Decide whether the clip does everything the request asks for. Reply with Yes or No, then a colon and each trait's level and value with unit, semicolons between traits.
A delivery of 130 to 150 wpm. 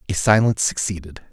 Yes: slow, 135 wpm